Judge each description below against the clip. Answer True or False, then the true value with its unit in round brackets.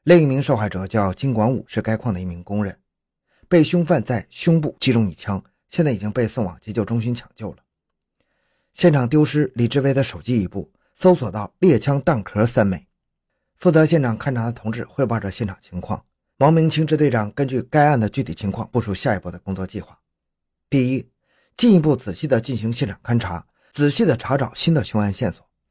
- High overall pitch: False (120 Hz)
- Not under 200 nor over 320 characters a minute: True (300 characters per minute)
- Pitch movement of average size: False (5.7 semitones)